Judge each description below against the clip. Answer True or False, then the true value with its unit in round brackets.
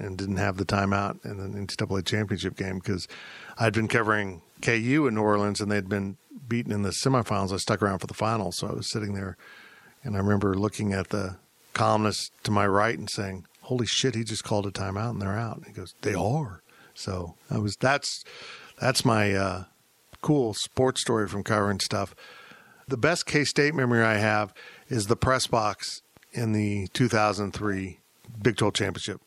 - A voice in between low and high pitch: False (105 Hz)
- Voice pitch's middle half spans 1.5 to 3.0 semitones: True (2.7 semitones)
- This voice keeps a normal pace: True (195 wpm)